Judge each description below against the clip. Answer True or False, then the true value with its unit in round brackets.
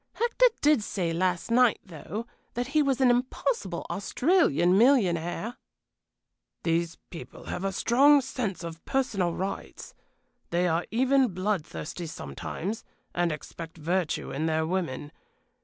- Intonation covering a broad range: True (6.9 semitones)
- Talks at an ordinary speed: False (130 wpm)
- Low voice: False (190 Hz)